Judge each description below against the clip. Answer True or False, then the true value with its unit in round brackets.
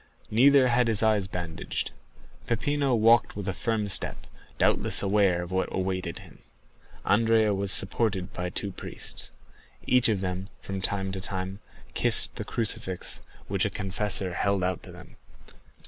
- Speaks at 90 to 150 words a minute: True (145 wpm)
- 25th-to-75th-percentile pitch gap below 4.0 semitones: True (3.2 semitones)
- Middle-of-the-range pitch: False (100 Hz)